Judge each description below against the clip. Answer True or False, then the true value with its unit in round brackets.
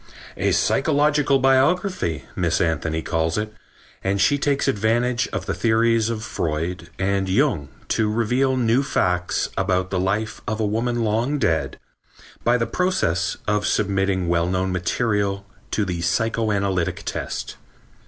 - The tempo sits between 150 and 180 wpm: False (140 wpm)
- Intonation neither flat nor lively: True (4.8 semitones)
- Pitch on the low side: True (105 Hz)